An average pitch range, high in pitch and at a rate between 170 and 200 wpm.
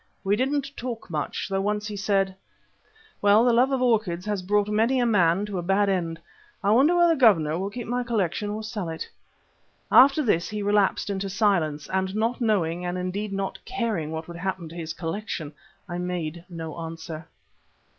Yes: average, 4.2 semitones; high, 195 Hz; average, 190 wpm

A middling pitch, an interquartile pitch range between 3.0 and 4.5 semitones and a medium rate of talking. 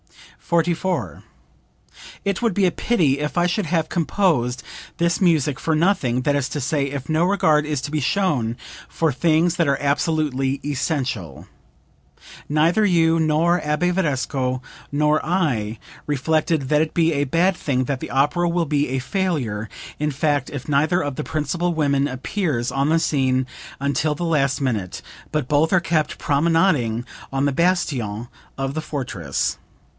Yes: medium, 150 Hz; average, 3.7 semitones; average, 160 wpm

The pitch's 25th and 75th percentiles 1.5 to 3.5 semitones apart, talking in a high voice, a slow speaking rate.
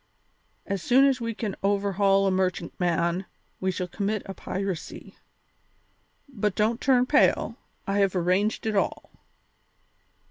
Yes: average, 2.7 semitones; high, 195 Hz; slow, 130 wpm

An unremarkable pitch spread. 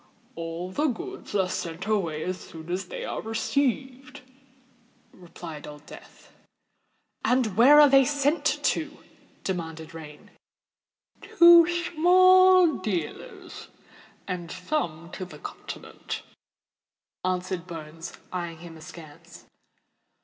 No: wide, 8.9 semitones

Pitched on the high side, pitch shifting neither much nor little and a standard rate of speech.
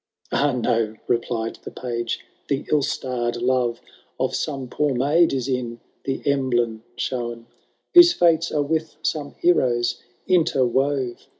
No: low, 130 Hz; average, 3.5 semitones; average, 160 wpm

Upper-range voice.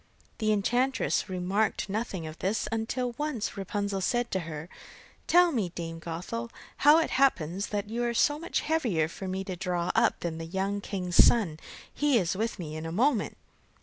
Yes: high, 200 Hz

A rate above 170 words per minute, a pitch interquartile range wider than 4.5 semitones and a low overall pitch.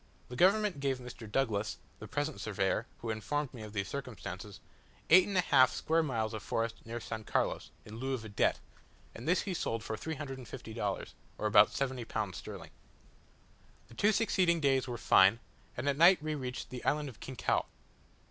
Yes: average, 185 wpm; average, 5.2 semitones; low, 130 Hz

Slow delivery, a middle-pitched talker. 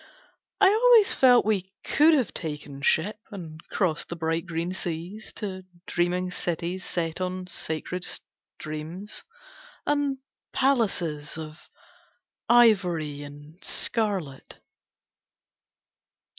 Yes: slow, 100 wpm; medium, 180 Hz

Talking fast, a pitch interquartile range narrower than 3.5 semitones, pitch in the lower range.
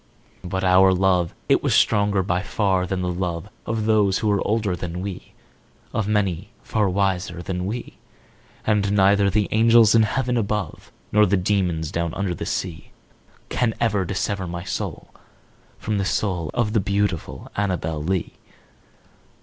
No: average, 155 wpm; narrow, 2.6 semitones; very low, 95 Hz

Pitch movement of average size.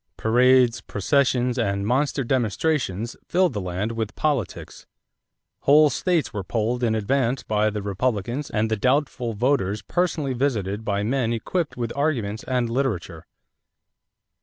Yes: average, 4.4 semitones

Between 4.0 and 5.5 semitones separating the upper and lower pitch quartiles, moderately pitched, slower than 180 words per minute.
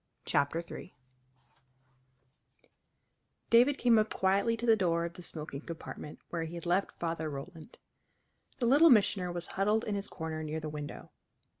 Yes: average, 5.1 semitones; medium, 175 Hz; average, 155 wpm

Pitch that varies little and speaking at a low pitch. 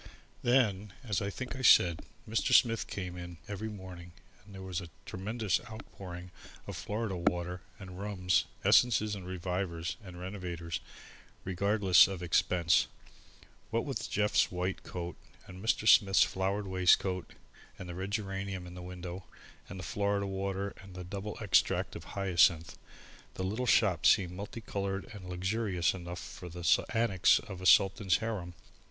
Yes: narrow, 2.3 semitones; very low, 95 Hz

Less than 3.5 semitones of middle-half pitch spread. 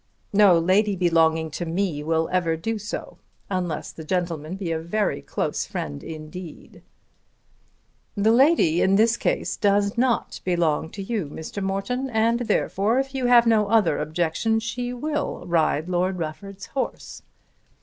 No: wide, 5.4 semitones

